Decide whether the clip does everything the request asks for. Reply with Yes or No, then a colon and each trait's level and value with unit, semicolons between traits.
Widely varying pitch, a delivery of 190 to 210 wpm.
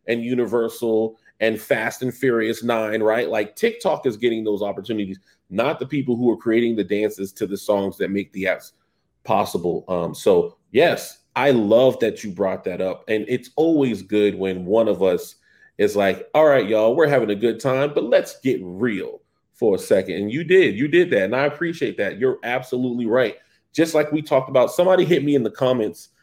Yes: wide, 7.0 semitones; fast, 205 wpm